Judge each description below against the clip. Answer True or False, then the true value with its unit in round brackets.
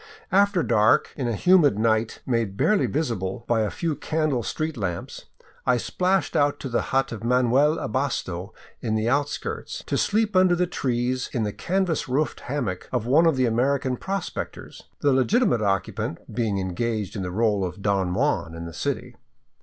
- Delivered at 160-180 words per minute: True (175 wpm)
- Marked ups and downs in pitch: True (6.3 semitones)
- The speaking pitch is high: False (125 Hz)